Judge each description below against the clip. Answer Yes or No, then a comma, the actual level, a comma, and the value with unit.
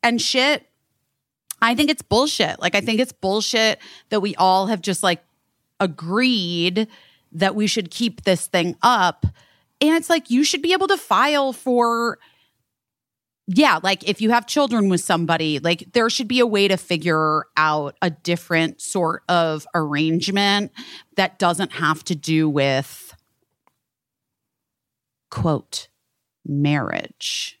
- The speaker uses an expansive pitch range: Yes, wide, 6.3 semitones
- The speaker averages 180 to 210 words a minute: No, average, 140 wpm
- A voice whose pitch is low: No, high, 190 Hz